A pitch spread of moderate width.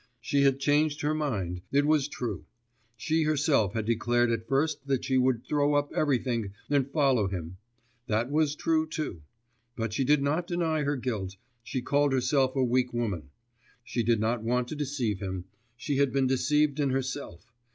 Yes: average, 3.9 semitones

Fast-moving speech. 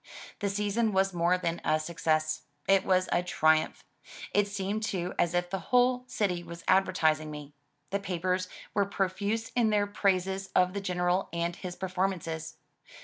No: average, 160 wpm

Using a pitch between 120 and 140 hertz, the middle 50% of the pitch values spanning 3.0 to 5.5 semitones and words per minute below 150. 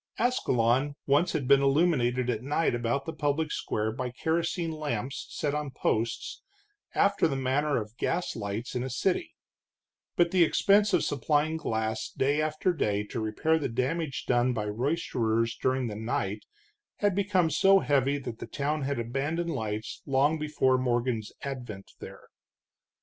No: low, 135 Hz; average, 4.9 semitones; average, 155 wpm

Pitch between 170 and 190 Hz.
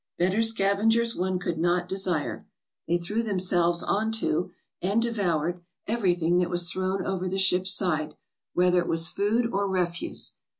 Yes: medium, 185 Hz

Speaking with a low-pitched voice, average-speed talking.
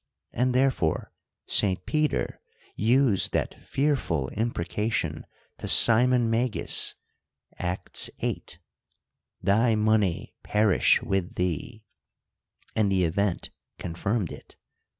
No: low, 105 Hz; slow, 95 wpm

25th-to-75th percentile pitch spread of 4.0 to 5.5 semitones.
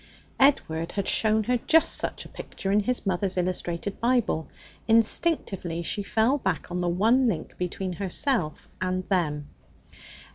Yes: average, 4.5 semitones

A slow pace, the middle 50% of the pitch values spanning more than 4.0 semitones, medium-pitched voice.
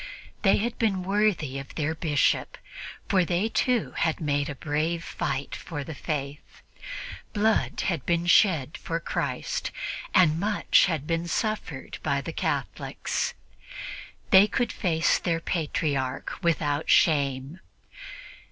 Yes: slow, 125 wpm; average, 4.5 semitones; medium, 165 Hz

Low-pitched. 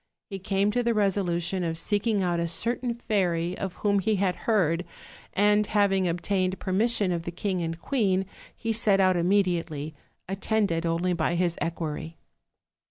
No: medium, 185 Hz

